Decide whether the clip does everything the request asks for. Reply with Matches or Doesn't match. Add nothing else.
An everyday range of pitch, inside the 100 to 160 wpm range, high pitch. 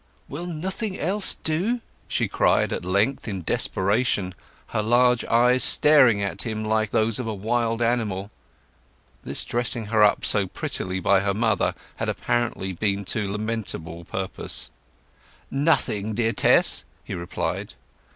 Doesn't match